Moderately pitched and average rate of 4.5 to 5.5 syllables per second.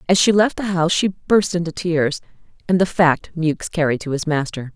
Yes: medium, 170 Hz; 5.2 syllables/s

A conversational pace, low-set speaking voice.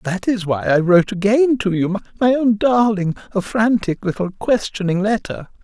No: average, 160 wpm; high, 205 Hz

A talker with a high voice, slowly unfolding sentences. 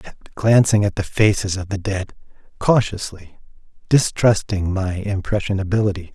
No: low, 100 Hz; slow, 125 wpm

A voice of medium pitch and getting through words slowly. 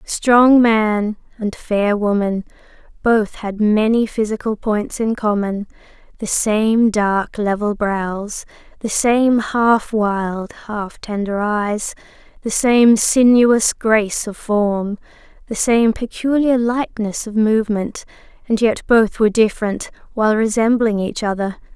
No: high, 215 Hz; slow, 110 wpm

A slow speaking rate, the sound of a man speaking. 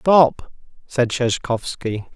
Yes: slow, 85 wpm; male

